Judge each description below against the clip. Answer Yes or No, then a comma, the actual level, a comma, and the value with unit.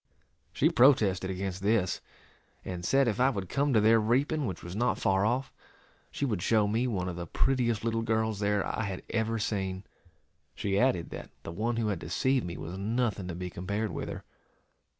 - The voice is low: Yes, low, 105 Hz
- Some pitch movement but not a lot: Yes, average, 3.9 semitones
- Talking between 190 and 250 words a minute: Yes, average, 195 wpm